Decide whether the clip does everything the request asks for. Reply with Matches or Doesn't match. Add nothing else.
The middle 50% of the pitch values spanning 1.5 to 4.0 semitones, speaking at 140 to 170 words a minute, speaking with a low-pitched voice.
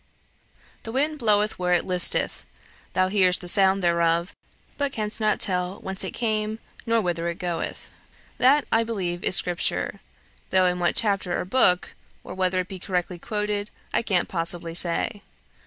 Doesn't match